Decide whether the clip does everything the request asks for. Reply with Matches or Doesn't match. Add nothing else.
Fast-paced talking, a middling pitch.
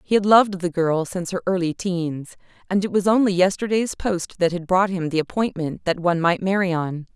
Matches